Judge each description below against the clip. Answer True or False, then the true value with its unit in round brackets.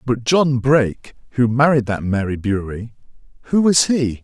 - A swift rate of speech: False (140 wpm)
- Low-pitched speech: True (125 Hz)